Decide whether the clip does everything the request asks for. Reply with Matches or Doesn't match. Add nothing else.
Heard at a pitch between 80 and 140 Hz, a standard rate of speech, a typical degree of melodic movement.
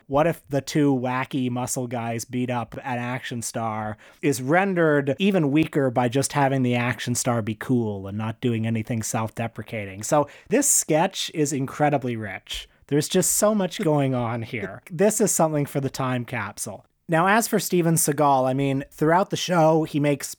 Matches